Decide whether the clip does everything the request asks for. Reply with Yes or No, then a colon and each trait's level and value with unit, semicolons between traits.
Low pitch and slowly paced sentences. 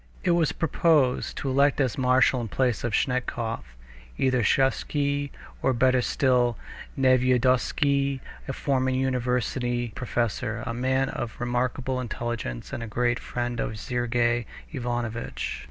Yes: low, 125 Hz; slow, 125 wpm